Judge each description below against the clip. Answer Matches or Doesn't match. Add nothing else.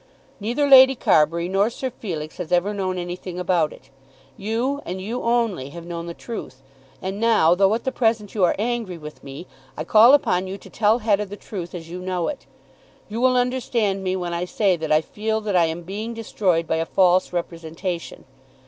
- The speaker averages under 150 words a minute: Doesn't match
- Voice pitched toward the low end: Doesn't match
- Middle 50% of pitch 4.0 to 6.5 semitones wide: Matches